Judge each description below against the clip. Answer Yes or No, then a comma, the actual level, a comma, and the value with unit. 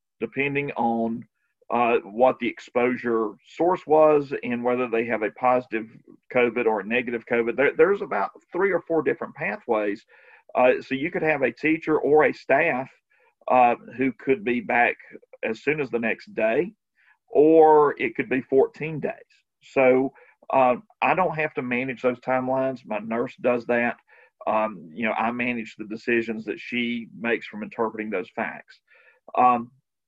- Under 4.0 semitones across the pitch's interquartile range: Yes, average, 2.8 semitones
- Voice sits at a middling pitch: No, low, 125 Hz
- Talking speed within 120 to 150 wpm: No, average, 165 wpm